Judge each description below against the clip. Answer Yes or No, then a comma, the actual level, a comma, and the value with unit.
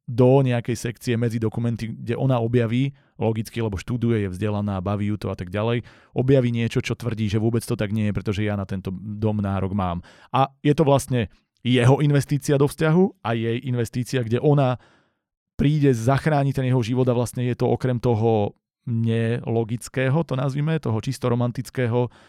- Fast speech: Yes, fast, 180 wpm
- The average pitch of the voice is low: Yes, low, 120 Hz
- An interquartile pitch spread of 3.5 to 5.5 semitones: No, average, 2.8 semitones